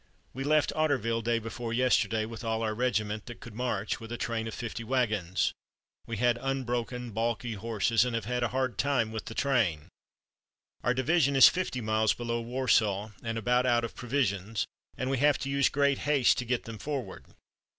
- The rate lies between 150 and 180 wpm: No, average, 190 wpm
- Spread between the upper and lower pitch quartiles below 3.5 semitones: Yes, narrow, 2.5 semitones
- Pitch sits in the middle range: No, low, 120 Hz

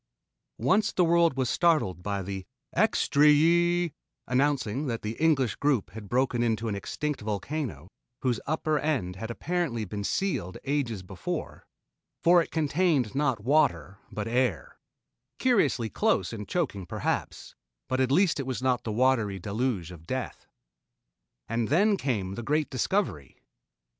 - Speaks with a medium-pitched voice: No, low, 130 Hz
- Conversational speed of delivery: Yes, average, 150 wpm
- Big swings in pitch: Yes, wide, 6.6 semitones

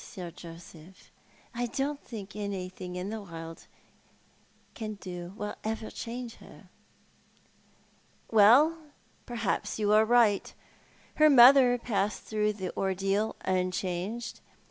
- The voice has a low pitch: No, high, 210 Hz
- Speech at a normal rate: No, slow, 110 wpm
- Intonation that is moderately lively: Yes, average, 4.1 semitones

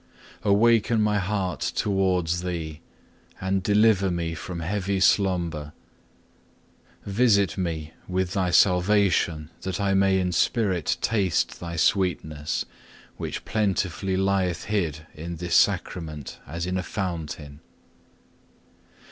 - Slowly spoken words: Yes, slow, 110 wpm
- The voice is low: Yes, very low, 90 Hz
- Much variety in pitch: No, average, 2.8 semitones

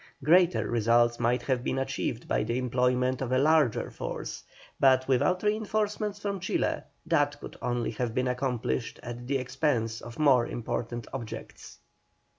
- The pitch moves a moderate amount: Yes, average, 3.5 semitones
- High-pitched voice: No, low, 125 Hz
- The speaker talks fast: No, average, 150 wpm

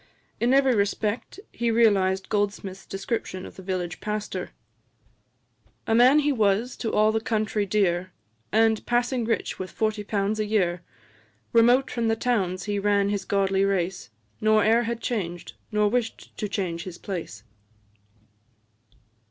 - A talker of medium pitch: No, high, 210 Hz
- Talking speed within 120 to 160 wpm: Yes, average, 145 wpm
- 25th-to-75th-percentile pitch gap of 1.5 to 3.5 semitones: Yes, average, 2.8 semitones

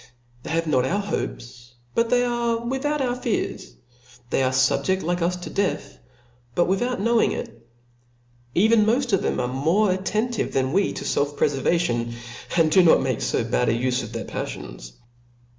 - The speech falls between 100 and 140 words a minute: No, average, 175 wpm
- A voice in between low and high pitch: Yes, medium, 175 Hz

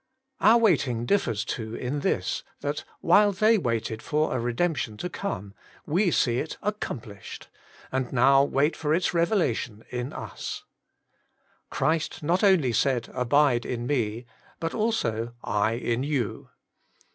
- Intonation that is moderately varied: No, wide, 6.2 semitones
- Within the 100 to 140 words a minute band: Yes, slow, 135 wpm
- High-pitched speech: No, low, 135 Hz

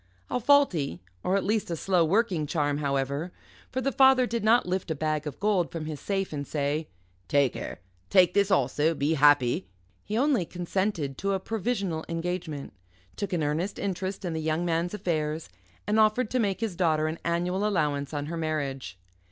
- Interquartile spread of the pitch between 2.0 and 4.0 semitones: No, average, 4.9 semitones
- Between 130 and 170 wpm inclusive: No, average, 185 wpm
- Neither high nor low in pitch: Yes, medium, 170 Hz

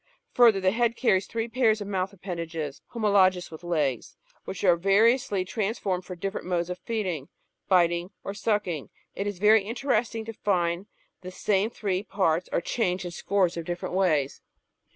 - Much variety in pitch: No, average, 3.4 semitones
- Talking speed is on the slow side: No, average, 170 wpm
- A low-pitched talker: No, high, 190 Hz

